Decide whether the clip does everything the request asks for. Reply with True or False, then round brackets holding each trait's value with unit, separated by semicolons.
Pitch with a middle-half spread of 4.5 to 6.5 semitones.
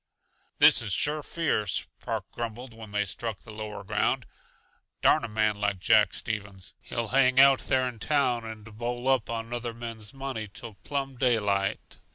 False (3.2 semitones)